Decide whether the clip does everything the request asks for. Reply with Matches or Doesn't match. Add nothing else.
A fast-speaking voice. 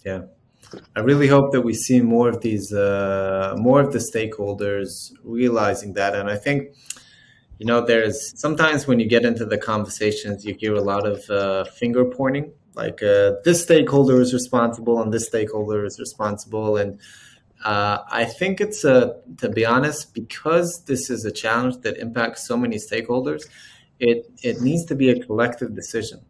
Doesn't match